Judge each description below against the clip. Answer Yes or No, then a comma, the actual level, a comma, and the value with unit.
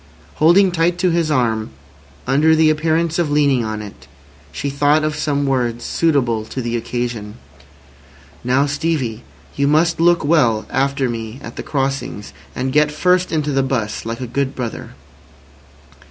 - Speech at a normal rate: Yes, average, 155 wpm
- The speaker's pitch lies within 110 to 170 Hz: Yes, medium, 140 Hz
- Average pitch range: Yes, average, 4.7 semitones